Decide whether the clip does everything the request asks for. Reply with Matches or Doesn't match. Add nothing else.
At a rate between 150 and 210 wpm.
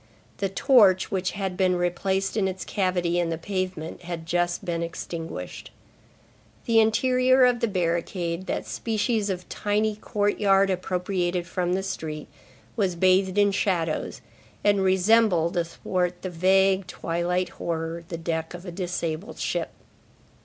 Doesn't match